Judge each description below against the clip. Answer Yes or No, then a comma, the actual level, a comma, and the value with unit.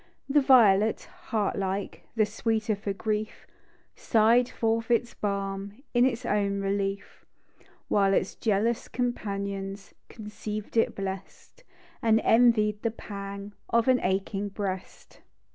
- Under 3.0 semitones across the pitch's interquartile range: Yes, narrow, 2.5 semitones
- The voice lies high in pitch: Yes, high, 210 Hz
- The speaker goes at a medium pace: No, slow, 120 wpm